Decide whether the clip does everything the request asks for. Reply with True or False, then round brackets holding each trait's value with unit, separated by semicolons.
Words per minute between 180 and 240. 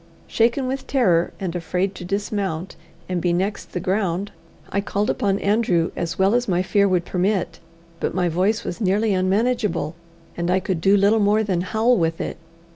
True (185 wpm)